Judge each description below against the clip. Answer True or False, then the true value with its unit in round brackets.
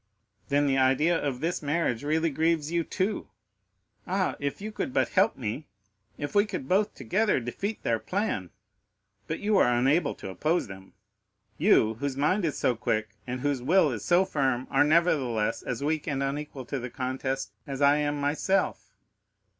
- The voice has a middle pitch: True (145 Hz)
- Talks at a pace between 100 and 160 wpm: False (170 wpm)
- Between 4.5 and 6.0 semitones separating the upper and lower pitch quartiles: True (5.1 semitones)